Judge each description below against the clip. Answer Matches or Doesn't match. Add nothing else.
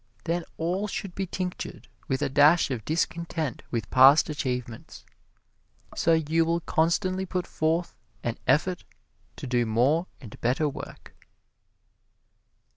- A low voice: Doesn't match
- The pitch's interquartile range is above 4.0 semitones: Matches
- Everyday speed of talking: Doesn't match